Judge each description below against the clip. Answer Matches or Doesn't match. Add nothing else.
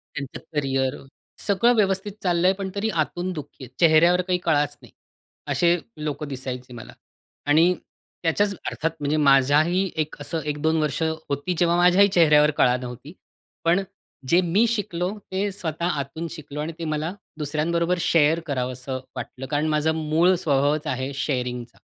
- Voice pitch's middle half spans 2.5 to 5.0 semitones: Matches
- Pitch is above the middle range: Doesn't match